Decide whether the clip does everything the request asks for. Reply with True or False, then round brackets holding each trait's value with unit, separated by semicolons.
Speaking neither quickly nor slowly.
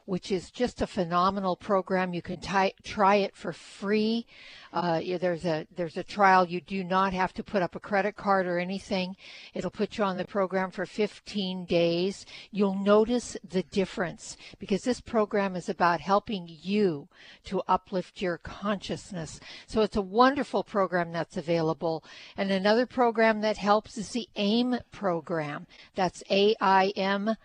True (160 wpm)